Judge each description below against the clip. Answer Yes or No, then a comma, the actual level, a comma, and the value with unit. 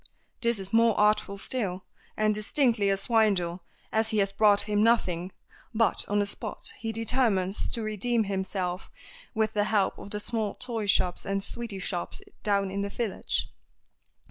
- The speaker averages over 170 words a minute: No, average, 165 wpm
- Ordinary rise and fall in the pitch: No, narrow, 2.2 semitones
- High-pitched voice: Yes, high, 205 Hz